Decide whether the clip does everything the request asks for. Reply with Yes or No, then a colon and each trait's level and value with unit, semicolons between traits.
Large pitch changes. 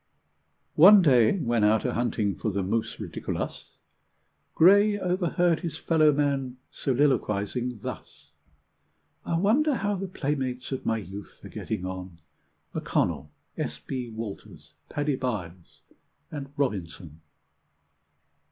Yes: wide, 7.7 semitones